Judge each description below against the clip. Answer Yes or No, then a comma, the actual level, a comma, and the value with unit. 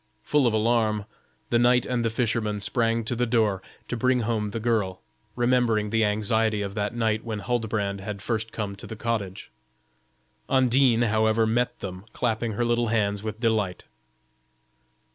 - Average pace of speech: Yes, average, 160 wpm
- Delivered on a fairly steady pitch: Yes, narrow, 2.1 semitones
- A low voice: Yes, low, 110 Hz